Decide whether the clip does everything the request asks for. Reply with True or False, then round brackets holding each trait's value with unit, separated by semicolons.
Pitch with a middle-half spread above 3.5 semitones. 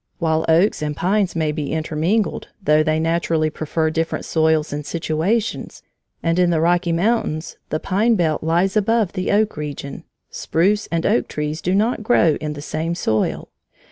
False (3.2 semitones)